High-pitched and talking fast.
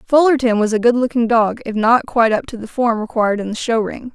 Yes: high, 230 Hz; fast, 260 wpm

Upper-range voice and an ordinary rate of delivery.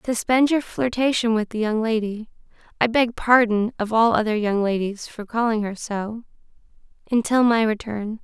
Yes: high, 225 Hz; average, 160 wpm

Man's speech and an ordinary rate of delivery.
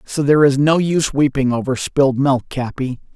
Yes: male; average, 190 wpm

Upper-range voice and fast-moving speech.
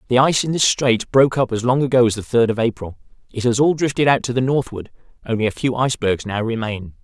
No: low, 120 Hz; fast, 245 wpm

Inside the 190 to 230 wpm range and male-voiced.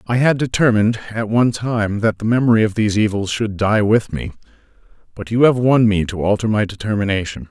Yes: average, 200 wpm; male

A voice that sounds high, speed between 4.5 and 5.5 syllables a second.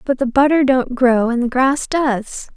No: very high, 260 Hz; 4.2 syllables/s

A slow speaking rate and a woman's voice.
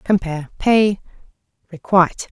Yes: slow, 75 wpm; female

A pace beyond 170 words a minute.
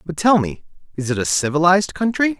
Yes: average, 200 wpm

